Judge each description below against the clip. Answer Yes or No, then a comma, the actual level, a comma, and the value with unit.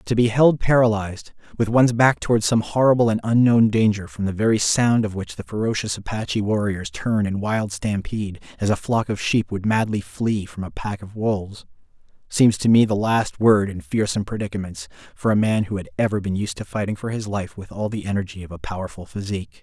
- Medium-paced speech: No, fast, 215 wpm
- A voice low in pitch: Yes, low, 105 Hz